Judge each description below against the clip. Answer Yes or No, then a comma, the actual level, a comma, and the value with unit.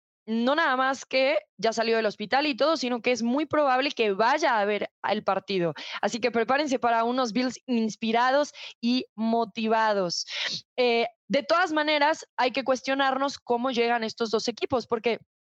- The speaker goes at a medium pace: Yes, average, 165 wpm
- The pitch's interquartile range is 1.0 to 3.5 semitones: Yes, average, 3.2 semitones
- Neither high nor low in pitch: No, high, 245 Hz